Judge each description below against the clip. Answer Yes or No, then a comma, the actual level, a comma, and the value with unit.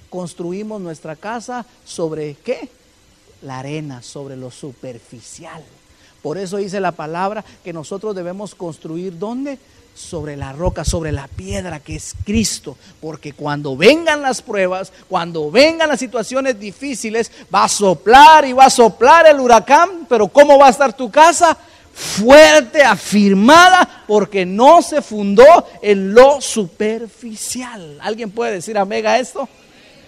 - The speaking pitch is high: Yes, high, 215 Hz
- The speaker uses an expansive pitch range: Yes, wide, 7.2 semitones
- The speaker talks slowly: No, average, 140 wpm